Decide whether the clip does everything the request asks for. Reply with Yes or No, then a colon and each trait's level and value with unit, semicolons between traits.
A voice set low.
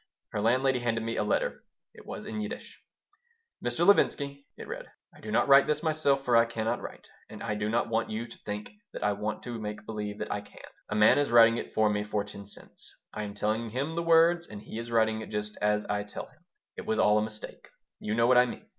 Yes: low, 115 Hz